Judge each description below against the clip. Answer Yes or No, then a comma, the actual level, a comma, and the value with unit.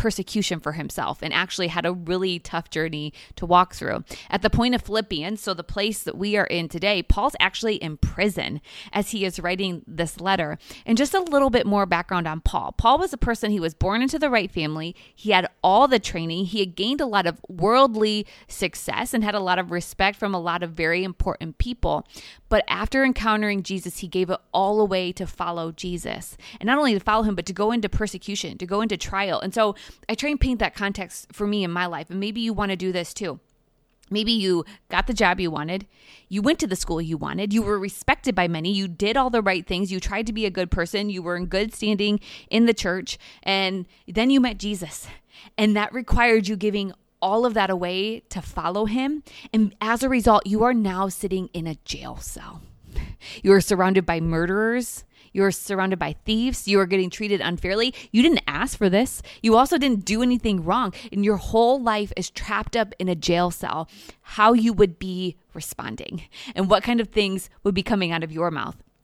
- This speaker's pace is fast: Yes, fast, 220 wpm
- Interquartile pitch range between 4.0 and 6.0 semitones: No, average, 3.6 semitones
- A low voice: No, high, 195 Hz